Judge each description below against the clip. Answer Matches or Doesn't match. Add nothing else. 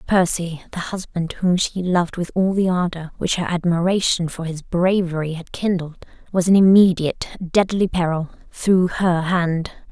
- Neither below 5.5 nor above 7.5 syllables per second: Doesn't match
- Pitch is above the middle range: Doesn't match